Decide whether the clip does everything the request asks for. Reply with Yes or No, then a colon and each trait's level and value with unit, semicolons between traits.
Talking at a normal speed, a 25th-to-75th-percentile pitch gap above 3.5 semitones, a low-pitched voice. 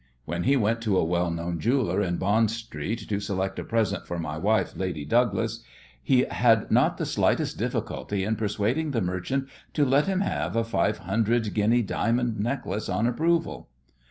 Yes: average, 180 wpm; average, 3.9 semitones; low, 110 Hz